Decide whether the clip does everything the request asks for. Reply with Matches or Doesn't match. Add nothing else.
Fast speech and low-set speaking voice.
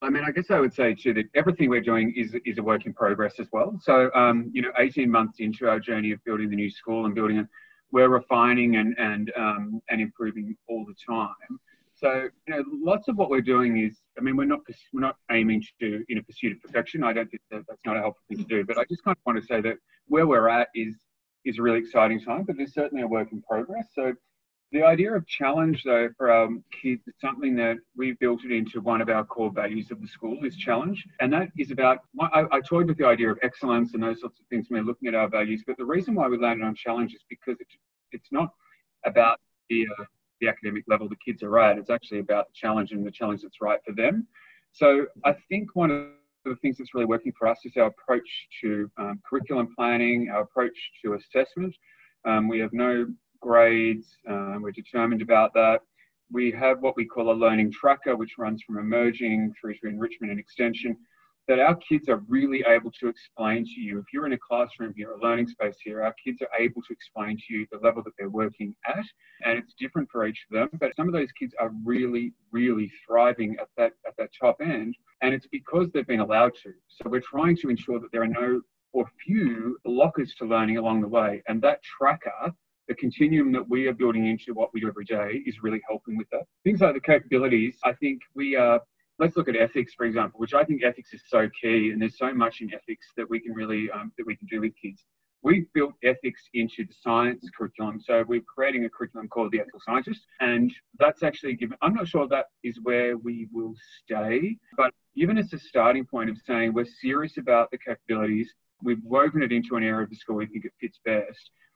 Matches